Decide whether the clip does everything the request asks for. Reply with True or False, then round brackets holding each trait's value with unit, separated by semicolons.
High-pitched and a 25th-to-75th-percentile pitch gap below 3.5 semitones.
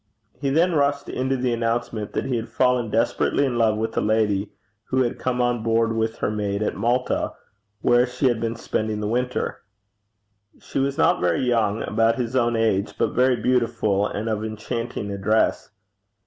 False (115 Hz; 2.6 semitones)